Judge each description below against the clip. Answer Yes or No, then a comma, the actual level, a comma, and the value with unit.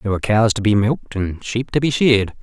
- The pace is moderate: No, fast, 275 wpm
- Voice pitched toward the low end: Yes, low, 110 Hz